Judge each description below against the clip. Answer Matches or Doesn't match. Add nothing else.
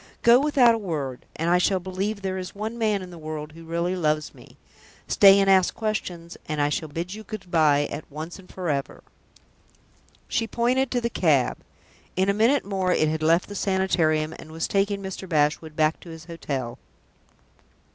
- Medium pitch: Matches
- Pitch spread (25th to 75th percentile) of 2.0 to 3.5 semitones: Doesn't match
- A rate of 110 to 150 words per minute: Doesn't match